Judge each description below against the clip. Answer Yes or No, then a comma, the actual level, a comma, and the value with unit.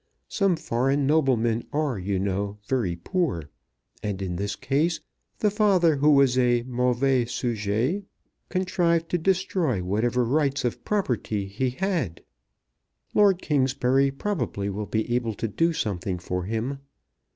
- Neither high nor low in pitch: No, low, 125 Hz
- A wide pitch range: Yes, wide, 7.2 semitones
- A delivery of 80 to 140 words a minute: Yes, slow, 135 wpm